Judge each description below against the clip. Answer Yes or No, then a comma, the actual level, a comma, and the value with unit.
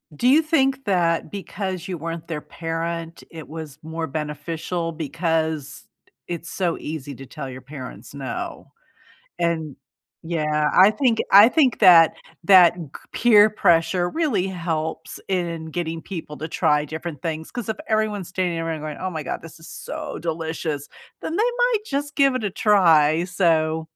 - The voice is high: No, medium, 165 Hz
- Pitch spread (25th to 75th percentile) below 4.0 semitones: Yes, average, 3.6 semitones